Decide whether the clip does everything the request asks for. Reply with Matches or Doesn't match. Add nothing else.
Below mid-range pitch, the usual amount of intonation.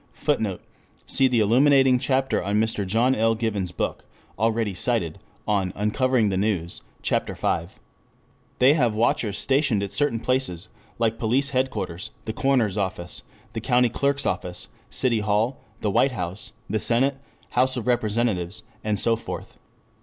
Matches